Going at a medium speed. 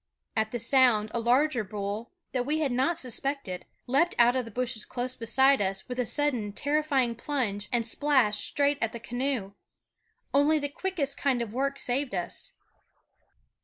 Yes: average, 165 wpm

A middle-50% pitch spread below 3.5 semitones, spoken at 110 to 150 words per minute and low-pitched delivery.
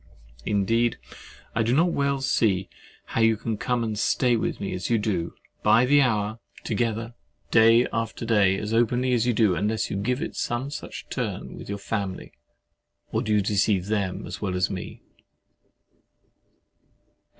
No: average, 2.8 semitones; average, 170 wpm; low, 110 Hz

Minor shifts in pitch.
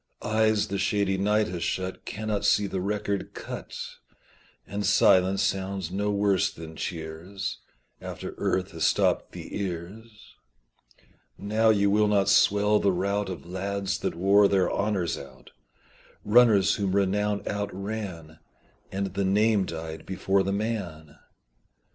Yes: narrow, 1.8 semitones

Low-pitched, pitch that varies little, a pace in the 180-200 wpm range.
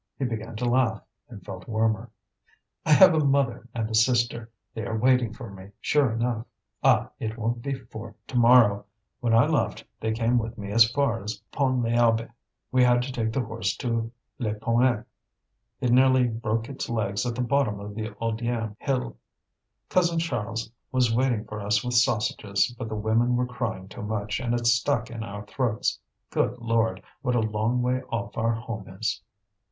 Yes: low, 115 Hz; narrow, 2.1 semitones; average, 185 wpm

